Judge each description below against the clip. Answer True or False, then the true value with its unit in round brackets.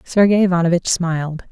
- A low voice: False (175 Hz)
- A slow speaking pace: True (120 wpm)